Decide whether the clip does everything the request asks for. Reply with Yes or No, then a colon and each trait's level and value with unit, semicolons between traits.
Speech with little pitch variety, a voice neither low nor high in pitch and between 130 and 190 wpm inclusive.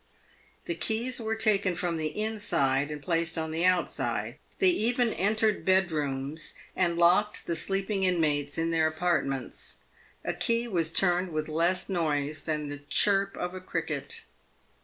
No: average, 4.3 semitones; medium, 175 Hz; average, 150 wpm